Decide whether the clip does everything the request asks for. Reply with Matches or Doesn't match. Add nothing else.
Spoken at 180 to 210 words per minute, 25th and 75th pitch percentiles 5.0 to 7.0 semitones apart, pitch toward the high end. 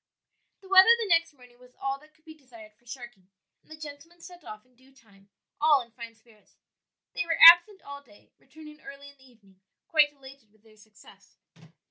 Matches